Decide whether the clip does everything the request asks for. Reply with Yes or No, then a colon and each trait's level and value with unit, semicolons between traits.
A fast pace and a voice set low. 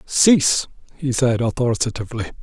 No: slow, 100 wpm; low, 125 Hz